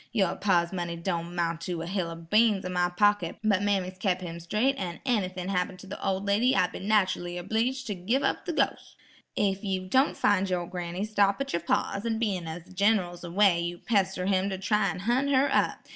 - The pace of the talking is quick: Yes, fast, 220 wpm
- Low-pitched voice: No, high, 190 Hz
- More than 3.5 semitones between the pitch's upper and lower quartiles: No, average, 3.0 semitones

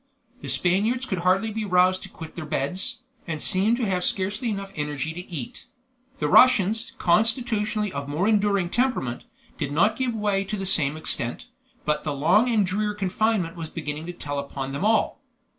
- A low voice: No, high, 190 Hz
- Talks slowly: No, average, 180 wpm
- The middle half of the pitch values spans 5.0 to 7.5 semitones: Yes, average, 5.3 semitones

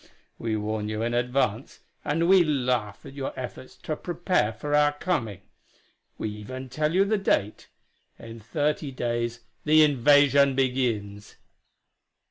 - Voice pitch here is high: No, low, 130 Hz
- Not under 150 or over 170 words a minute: No, slow, 135 wpm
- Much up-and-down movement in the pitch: No, average, 4.6 semitones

